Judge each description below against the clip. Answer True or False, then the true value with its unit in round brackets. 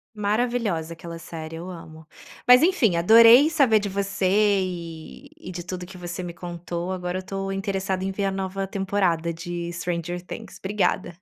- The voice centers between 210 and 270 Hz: False (185 Hz)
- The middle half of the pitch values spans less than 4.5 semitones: True (2.7 semitones)